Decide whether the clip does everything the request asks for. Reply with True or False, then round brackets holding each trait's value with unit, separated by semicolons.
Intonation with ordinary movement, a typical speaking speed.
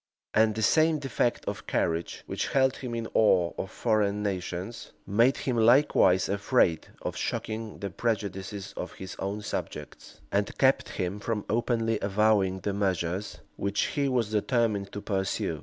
True (3.2 semitones; 155 wpm)